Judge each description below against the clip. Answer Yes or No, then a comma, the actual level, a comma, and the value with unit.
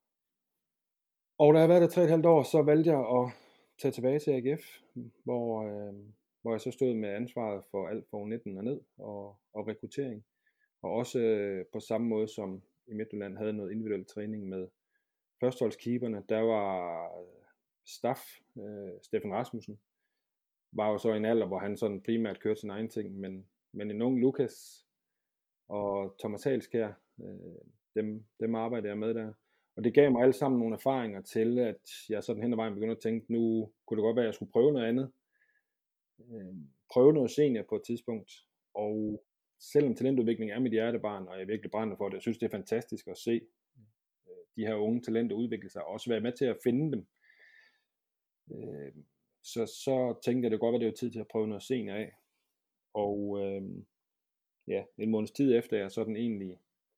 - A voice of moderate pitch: No, low, 110 Hz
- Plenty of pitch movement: No, average, 2.7 semitones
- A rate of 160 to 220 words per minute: Yes, average, 190 wpm